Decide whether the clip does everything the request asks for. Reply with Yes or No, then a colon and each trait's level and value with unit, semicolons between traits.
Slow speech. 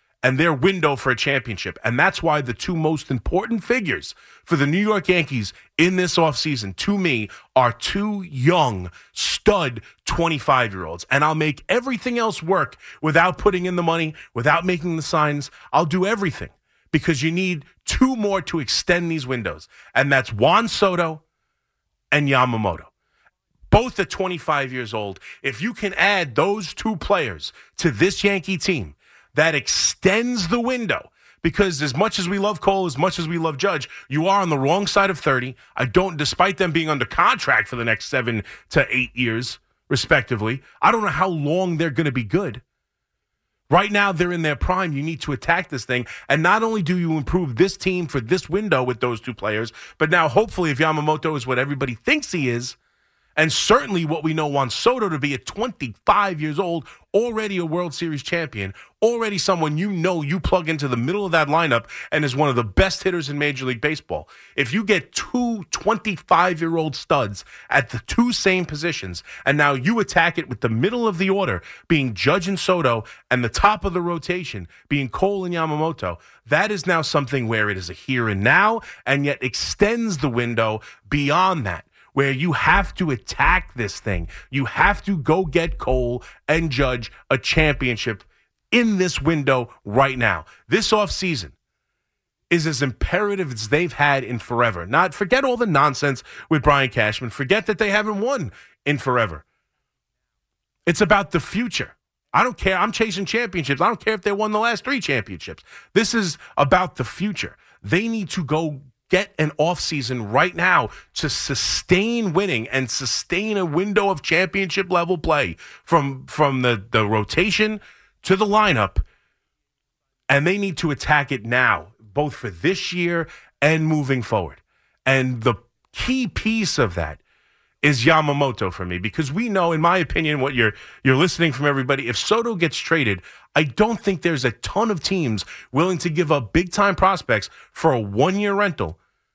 No: average, 185 wpm